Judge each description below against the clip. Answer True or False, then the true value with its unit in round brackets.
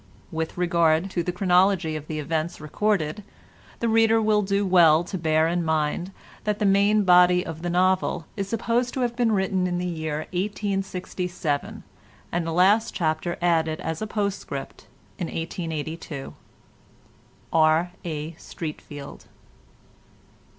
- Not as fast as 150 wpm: True (140 wpm)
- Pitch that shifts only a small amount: False (3.7 semitones)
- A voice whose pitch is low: False (175 Hz)